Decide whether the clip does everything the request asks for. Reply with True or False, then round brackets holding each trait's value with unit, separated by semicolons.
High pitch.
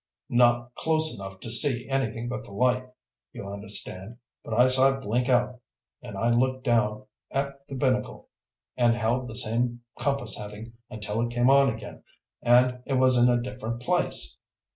False (120 Hz)